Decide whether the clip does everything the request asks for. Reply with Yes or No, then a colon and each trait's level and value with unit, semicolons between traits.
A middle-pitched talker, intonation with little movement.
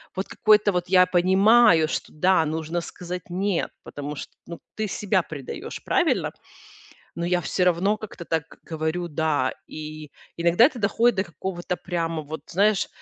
No: medium, 175 Hz; average, 3.2 semitones